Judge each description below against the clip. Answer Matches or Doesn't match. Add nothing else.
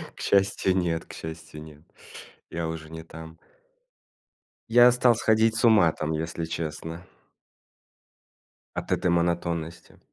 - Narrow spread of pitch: Doesn't match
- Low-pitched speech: Matches